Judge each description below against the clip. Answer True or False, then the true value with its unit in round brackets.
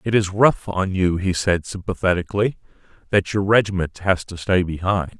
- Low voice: True (95 Hz)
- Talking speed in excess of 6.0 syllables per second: False (5.0 syllables/s)